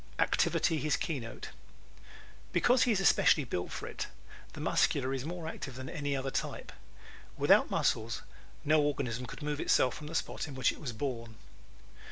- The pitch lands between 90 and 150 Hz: Yes, medium, 140 Hz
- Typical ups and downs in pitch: Yes, average, 3.5 semitones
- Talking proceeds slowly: No, average, 175 wpm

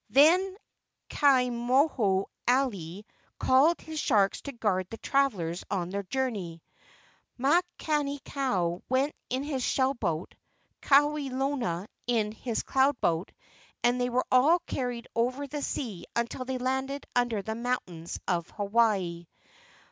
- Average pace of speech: No, slow, 125 wpm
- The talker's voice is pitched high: Yes, high, 245 Hz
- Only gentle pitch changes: No, wide, 5.5 semitones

